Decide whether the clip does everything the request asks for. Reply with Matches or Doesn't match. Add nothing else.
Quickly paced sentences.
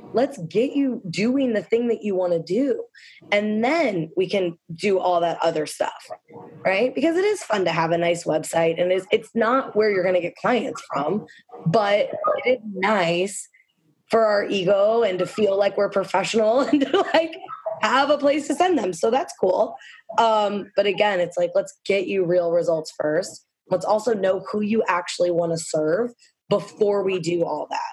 Doesn't match